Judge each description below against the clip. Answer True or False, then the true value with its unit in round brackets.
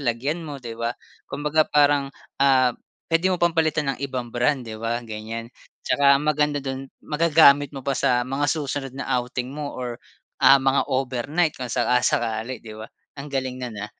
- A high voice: False (135 Hz)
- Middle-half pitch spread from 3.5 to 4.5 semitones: False (3.1 semitones)